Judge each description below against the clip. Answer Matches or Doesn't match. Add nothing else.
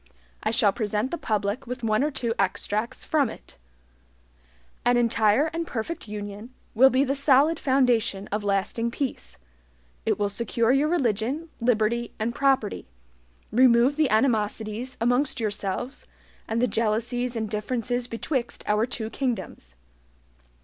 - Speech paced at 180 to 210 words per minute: Doesn't match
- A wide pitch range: Doesn't match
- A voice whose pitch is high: Matches